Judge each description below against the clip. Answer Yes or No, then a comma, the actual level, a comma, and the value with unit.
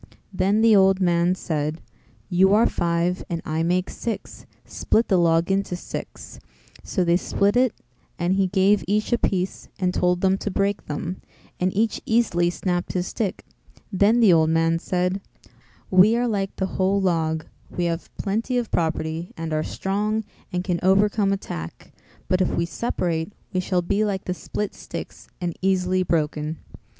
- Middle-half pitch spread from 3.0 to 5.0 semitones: No, narrow, 2.6 semitones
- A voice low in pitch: No, medium, 185 Hz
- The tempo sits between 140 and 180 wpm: Yes, average, 170 wpm